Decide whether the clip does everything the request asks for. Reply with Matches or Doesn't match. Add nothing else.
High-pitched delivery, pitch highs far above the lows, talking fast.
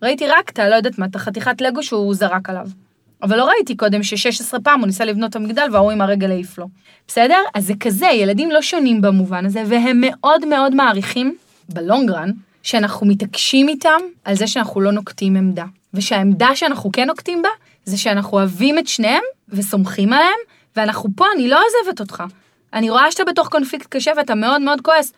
Matches